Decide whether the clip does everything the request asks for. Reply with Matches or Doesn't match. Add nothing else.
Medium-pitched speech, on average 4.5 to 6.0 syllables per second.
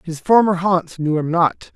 Doesn't match